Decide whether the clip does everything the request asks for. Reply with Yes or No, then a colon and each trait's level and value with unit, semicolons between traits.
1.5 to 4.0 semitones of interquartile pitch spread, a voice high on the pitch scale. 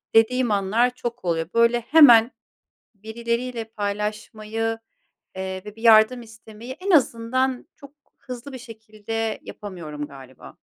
Yes: narrow, 2.4 semitones; high, 225 Hz